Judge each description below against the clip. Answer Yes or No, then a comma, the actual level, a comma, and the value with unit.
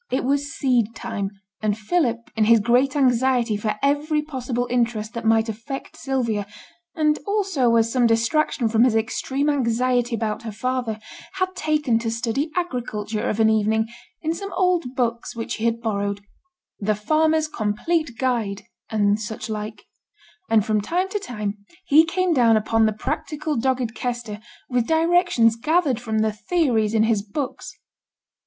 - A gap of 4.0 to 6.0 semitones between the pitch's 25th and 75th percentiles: Yes, average, 4.5 semitones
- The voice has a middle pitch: No, high, 235 Hz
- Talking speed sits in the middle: Yes, average, 160 wpm